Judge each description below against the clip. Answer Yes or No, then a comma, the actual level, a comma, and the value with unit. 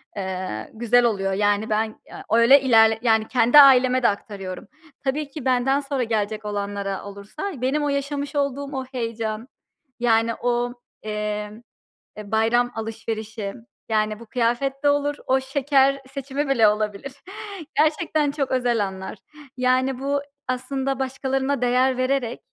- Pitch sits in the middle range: No, high, 245 Hz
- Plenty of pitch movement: No, average, 3.9 semitones